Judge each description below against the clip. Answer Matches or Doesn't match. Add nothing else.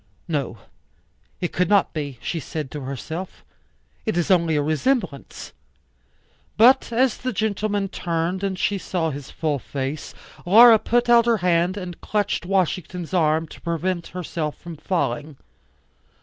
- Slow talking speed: Doesn't match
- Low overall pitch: Doesn't match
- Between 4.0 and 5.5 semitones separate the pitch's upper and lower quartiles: Matches